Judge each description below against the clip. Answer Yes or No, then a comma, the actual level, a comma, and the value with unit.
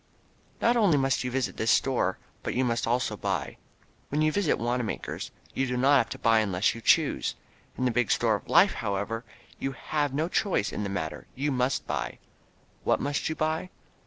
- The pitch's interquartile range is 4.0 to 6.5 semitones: Yes, average, 4.3 semitones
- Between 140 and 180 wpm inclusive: No, average, 195 wpm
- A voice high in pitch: No, low, 125 Hz